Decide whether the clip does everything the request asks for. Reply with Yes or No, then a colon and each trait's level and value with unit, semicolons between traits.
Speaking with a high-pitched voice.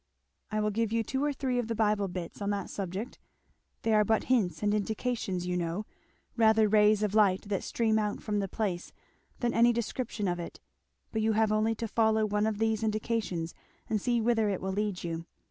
Yes: high, 215 Hz